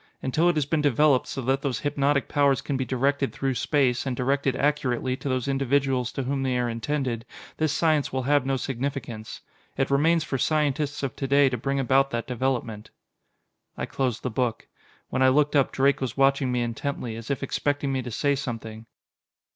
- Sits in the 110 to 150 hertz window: Yes, low, 135 Hz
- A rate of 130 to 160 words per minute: No, average, 195 wpm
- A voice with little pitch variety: Yes, narrow, 2.1 semitones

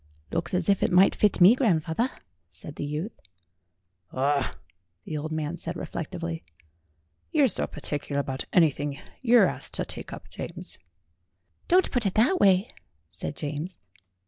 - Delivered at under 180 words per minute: Yes, average, 155 wpm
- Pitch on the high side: No, medium, 165 Hz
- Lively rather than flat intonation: Yes, wide, 5.7 semitones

